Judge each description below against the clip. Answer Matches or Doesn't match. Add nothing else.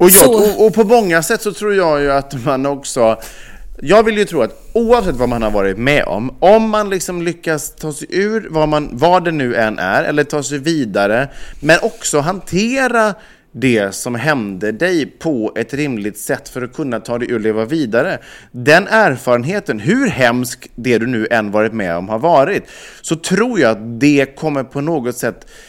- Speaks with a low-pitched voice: Doesn't match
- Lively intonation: Matches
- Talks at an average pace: Doesn't match